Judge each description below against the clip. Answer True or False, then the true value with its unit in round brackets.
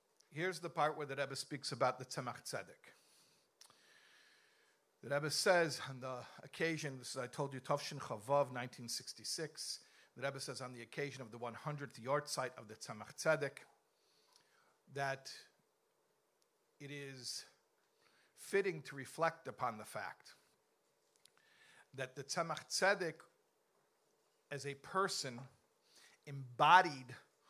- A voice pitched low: False (145 Hz)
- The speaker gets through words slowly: True (120 wpm)